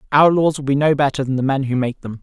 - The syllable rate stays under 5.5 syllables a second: No, 6.5 syllables/s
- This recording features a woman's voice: No, male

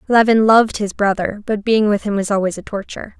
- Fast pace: Yes, fast, 225 wpm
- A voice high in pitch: Yes, high, 210 Hz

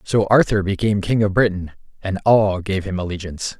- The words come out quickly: No, average, 185 wpm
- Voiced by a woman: No, male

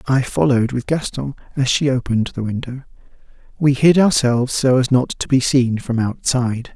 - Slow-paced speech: No, average, 180 wpm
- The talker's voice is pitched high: No, low, 130 Hz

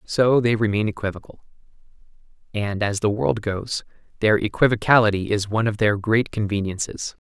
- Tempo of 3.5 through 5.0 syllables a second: No, 5.3 syllables/s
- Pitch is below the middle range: Yes, low, 105 Hz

